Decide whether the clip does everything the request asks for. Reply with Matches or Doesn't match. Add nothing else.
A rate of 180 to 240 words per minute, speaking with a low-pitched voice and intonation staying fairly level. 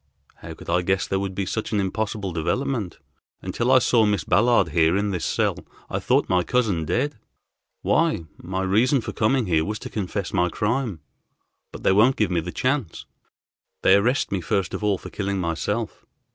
Doesn't match